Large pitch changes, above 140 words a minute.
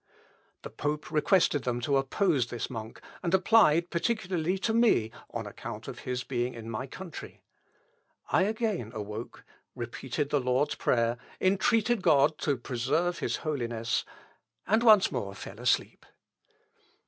No: wide, 7.7 semitones; slow, 135 wpm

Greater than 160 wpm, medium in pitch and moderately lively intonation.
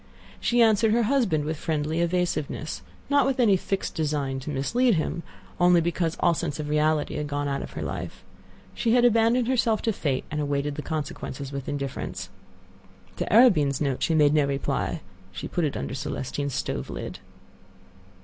No: average, 170 wpm; medium, 155 Hz; wide, 6.9 semitones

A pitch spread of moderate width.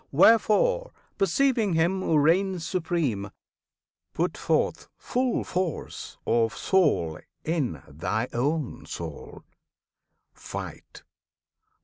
No: wide, 8.5 semitones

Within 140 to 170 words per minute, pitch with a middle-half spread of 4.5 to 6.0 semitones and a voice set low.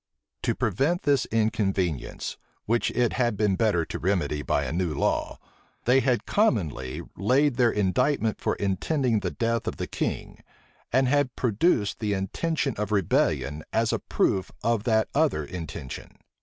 Yes: average, 155 wpm; average, 5.2 semitones; low, 110 Hz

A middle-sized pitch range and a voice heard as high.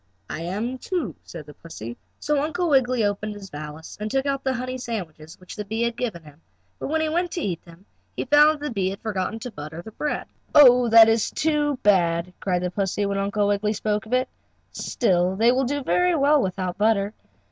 No: wide, 6.3 semitones; high, 215 Hz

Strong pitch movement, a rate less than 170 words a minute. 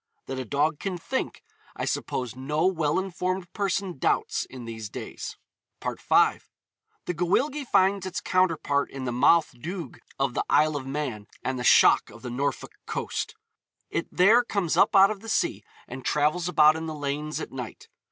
No: wide, 5.7 semitones; average, 175 wpm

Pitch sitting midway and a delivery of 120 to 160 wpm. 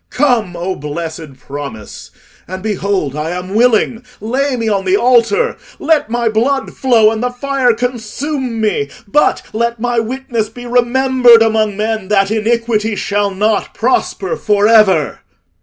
No: high, 225 Hz; average, 140 wpm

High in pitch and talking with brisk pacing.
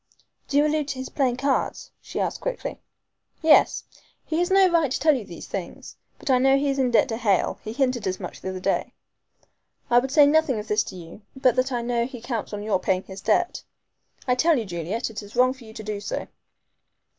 Yes: very high, 250 Hz; fast, 235 wpm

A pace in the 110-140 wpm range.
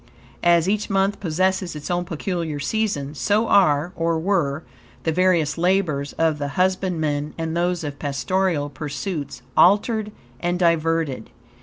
Yes: slow, 135 wpm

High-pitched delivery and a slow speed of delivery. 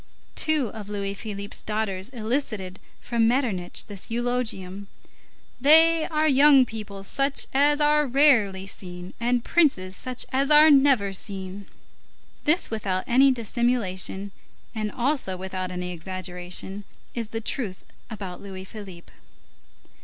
Yes: high, 215 Hz; slow, 125 wpm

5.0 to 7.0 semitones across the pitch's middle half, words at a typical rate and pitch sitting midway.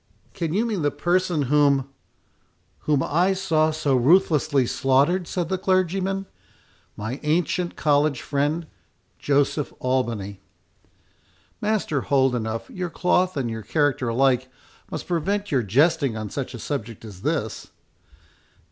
No: wide, 5.4 semitones; slow, 120 wpm; medium, 145 Hz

